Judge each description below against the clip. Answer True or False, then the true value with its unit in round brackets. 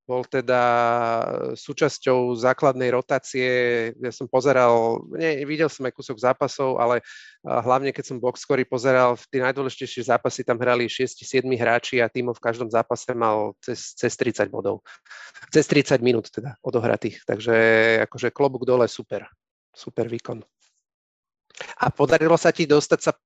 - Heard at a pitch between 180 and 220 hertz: False (125 Hz)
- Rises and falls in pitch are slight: True (2.0 semitones)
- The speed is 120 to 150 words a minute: True (145 wpm)